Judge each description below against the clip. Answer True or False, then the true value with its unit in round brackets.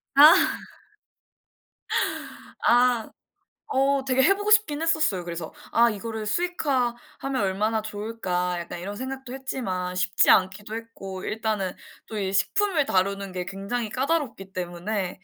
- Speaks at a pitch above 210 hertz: True (220 Hz)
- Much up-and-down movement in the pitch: True (5.8 semitones)